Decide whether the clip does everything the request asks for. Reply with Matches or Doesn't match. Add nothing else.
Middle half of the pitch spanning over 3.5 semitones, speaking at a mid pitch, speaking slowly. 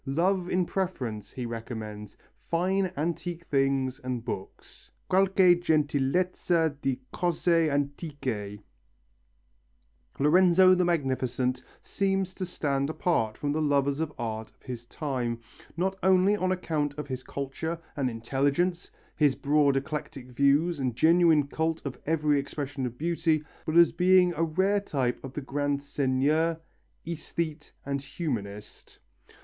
Matches